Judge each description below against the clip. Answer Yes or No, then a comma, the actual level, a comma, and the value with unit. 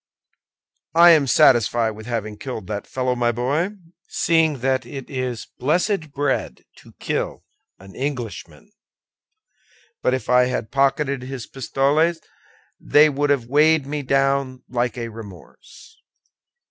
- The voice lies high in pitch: No, low, 130 Hz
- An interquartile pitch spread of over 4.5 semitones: No, average, 3.3 semitones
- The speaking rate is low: Yes, slow, 130 wpm